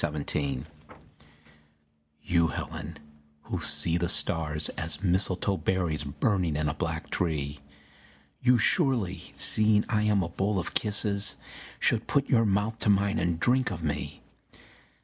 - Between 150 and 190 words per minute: No, average, 140 wpm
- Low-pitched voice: Yes, very low, 95 Hz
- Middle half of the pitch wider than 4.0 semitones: Yes, average, 4.6 semitones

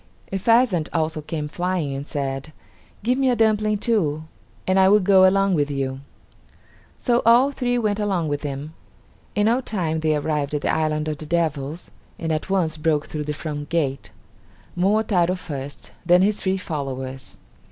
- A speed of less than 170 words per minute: No, average, 175 wpm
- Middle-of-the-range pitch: Yes, medium, 165 Hz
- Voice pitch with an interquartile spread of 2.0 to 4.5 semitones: No, average, 5.2 semitones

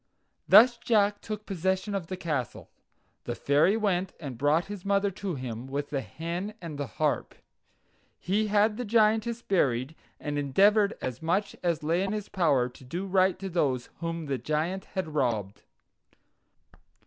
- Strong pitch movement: Yes, wide, 5.8 semitones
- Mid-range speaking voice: Yes, medium, 175 Hz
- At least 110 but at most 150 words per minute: No, average, 160 wpm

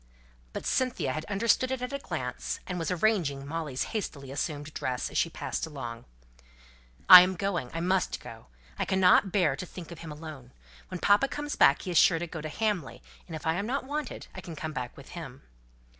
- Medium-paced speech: No, fast, 210 wpm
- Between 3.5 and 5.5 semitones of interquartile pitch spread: Yes, average, 5.2 semitones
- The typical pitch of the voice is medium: Yes, medium, 170 Hz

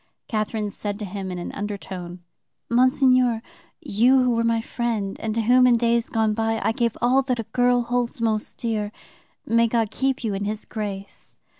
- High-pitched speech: Yes, high, 225 Hz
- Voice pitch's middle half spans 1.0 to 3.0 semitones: Yes, narrow, 2.6 semitones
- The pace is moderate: Yes, average, 185 wpm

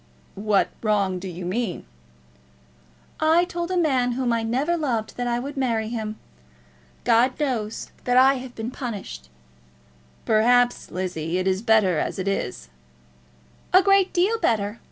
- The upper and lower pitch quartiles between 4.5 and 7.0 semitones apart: Yes, average, 4.8 semitones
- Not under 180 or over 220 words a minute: No, average, 150 wpm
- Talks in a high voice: Yes, high, 235 Hz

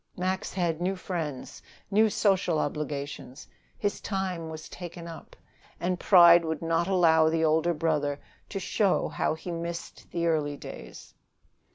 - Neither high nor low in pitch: Yes, medium, 170 Hz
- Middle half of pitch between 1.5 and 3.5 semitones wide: Yes, narrow, 2.5 semitones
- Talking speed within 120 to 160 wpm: Yes, average, 145 wpm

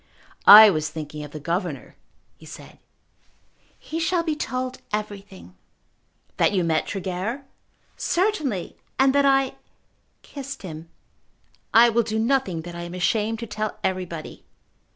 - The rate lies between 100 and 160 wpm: Yes, slow, 135 wpm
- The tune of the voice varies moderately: No, wide, 7.2 semitones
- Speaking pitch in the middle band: No, high, 210 Hz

